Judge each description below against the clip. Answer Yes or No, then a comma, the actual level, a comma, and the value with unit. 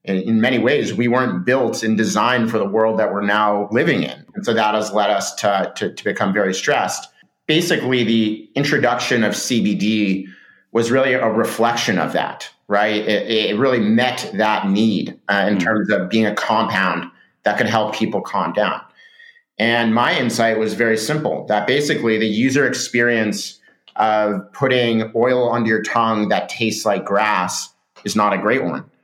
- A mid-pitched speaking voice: No, low, 110 Hz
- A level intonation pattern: Yes, narrow, 2.0 semitones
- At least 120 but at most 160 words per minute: No, average, 175 wpm